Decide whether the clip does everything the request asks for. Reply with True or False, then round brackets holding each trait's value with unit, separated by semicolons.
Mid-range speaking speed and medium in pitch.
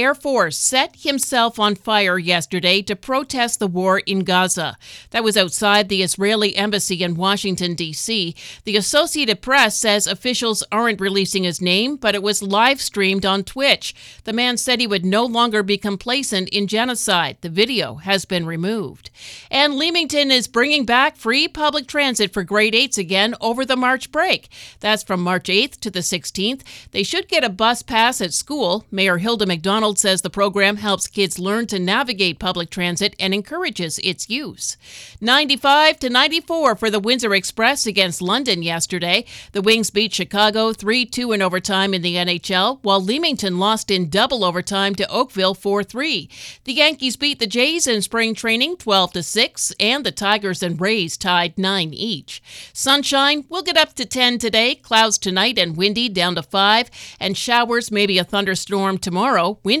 False (170 wpm; 210 Hz)